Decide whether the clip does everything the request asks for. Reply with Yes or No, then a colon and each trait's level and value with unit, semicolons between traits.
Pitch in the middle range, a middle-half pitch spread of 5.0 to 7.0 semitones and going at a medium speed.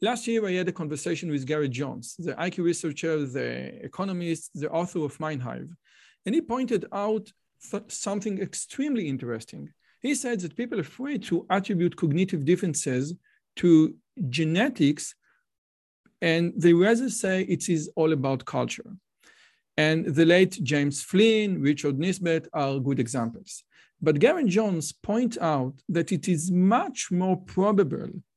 No: medium, 175 Hz; average, 4.6 semitones; average, 145 wpm